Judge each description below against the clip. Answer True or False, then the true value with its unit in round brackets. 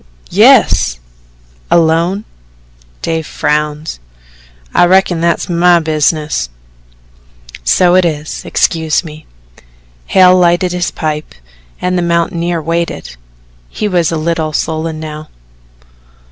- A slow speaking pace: True (105 wpm)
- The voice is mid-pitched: True (165 Hz)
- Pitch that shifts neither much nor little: False (2.1 semitones)